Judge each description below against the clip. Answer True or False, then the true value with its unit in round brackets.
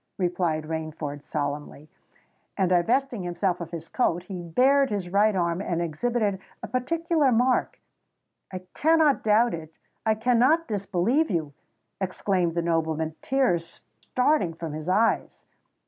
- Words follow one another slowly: True (130 wpm)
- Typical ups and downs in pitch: False (6.6 semitones)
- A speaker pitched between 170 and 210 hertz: True (185 Hz)